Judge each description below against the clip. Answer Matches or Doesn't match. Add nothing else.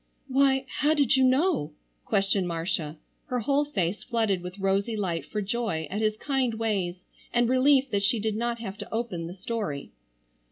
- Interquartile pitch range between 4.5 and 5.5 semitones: Matches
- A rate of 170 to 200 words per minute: Matches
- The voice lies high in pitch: Matches